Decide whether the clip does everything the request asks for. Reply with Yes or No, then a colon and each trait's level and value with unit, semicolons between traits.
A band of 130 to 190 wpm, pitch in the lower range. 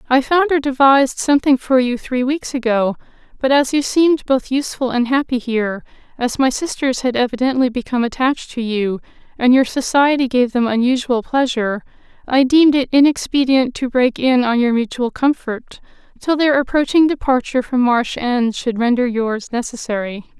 No: average, 160 wpm; very high, 255 Hz